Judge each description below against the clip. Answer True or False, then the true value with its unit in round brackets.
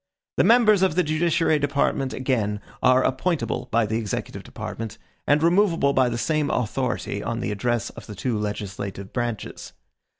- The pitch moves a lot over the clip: True (6.0 semitones)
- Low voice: True (130 Hz)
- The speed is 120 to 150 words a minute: False (160 wpm)